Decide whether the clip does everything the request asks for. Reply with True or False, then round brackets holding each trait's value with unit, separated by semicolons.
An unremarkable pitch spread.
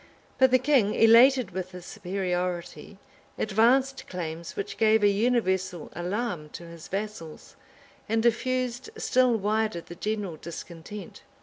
True (4.9 semitones)